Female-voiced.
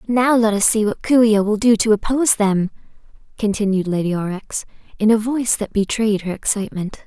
Yes: female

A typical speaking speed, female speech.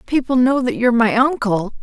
Yes: average, 195 wpm; female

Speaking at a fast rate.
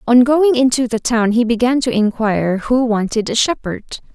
No: average, 190 wpm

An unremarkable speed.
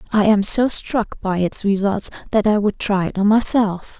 No: fast, 210 wpm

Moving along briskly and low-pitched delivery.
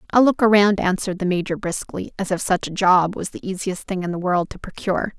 No: fast, 245 wpm; high, 190 Hz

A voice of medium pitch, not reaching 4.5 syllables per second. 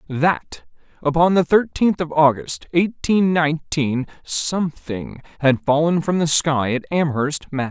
Yes: medium, 150 Hz; 4.0 syllables/s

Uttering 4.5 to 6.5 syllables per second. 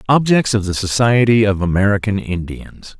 Yes: 5.0 syllables/s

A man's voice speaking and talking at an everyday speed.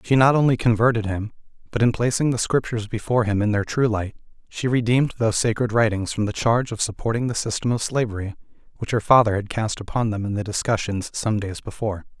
No: male; fast, 210 wpm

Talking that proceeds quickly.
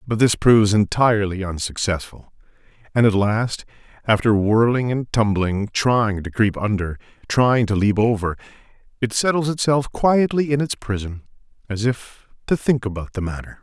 No: average, 150 wpm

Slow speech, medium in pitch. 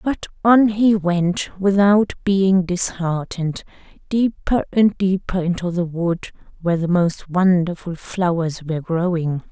Yes: slow, 125 wpm; medium, 180 Hz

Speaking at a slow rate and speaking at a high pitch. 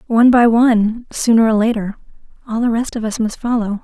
No: fast, 205 wpm; high, 225 Hz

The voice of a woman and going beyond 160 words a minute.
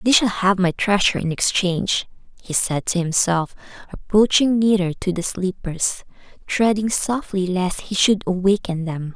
No: female; average, 150 wpm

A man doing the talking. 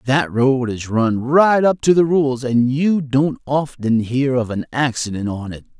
Yes: male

